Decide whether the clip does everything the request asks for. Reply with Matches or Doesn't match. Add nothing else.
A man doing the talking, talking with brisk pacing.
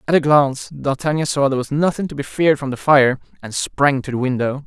Matches